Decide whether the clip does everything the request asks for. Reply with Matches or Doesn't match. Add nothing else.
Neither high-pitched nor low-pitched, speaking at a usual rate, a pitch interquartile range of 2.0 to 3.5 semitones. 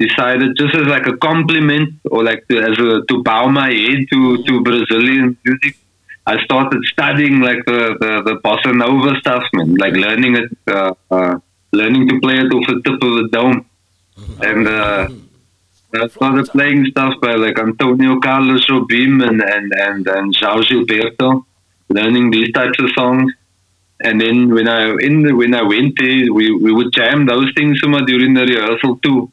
Doesn't match